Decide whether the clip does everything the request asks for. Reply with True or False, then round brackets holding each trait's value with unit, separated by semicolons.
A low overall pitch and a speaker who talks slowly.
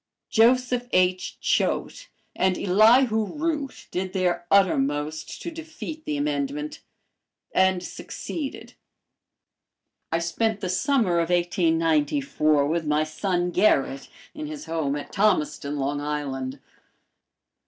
False (185 Hz; 110 wpm)